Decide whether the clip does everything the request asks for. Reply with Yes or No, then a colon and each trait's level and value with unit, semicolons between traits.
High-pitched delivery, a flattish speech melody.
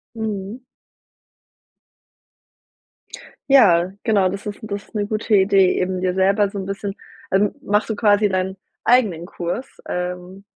Yes: high, 195 Hz; narrow, 2.1 semitones